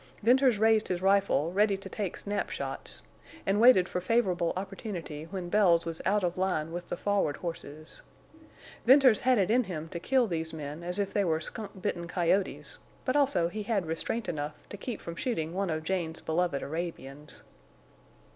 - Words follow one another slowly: No, average, 180 wpm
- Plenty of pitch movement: No, average, 4.0 semitones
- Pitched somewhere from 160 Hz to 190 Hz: Yes, medium, 185 Hz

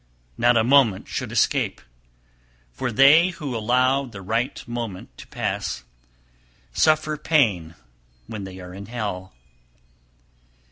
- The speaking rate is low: Yes, slow, 120 wpm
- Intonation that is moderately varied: No, wide, 5.9 semitones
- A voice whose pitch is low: Yes, low, 120 Hz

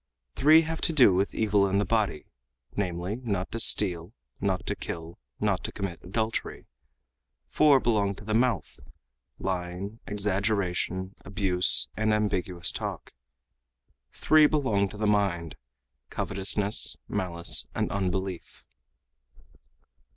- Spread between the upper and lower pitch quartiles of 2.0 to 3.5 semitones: Yes, average, 3.0 semitones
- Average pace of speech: No, slow, 120 wpm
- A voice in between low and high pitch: No, low, 100 Hz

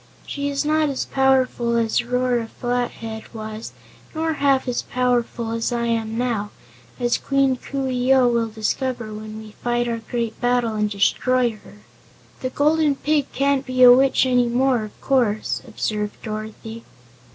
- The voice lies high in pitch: Yes, high, 245 Hz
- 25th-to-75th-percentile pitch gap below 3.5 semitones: Yes, average, 2.8 semitones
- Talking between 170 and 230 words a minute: No, average, 160 wpm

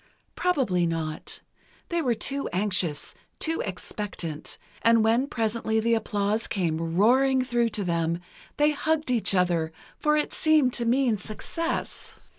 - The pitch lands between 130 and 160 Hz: No, high, 225 Hz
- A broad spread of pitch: Yes, wide, 6.7 semitones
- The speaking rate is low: Yes, slow, 130 wpm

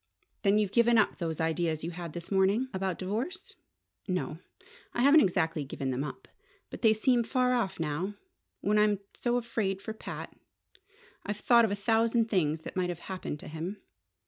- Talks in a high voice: Yes, high, 195 Hz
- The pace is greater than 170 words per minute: Yes, average, 180 wpm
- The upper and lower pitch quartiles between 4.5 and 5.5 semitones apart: Yes, average, 5.1 semitones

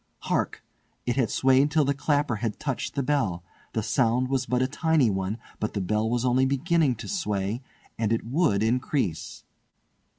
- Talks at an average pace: Yes, average, 175 wpm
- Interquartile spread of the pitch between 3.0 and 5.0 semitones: Yes, average, 4.3 semitones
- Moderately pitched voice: No, low, 125 Hz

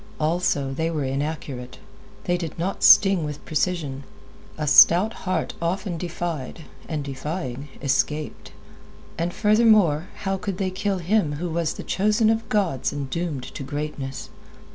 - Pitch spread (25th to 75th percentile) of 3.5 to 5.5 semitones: Yes, average, 4.3 semitones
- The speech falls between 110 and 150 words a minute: Yes, average, 140 wpm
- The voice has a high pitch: No, medium, 165 Hz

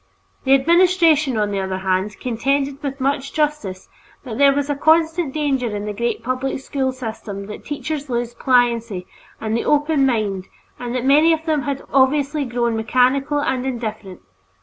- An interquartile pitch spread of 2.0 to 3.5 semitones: No, average, 4.1 semitones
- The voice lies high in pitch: Yes, very high, 260 Hz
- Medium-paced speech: Yes, average, 170 wpm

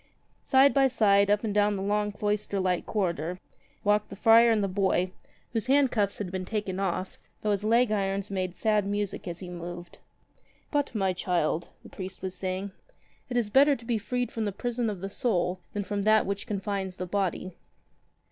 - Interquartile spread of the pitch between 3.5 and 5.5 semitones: No, narrow, 2.6 semitones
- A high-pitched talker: Yes, high, 200 Hz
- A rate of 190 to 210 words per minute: Yes, average, 200 wpm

